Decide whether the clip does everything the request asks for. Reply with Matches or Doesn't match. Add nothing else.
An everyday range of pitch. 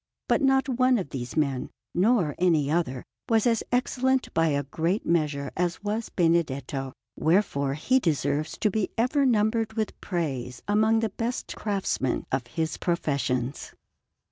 Doesn't match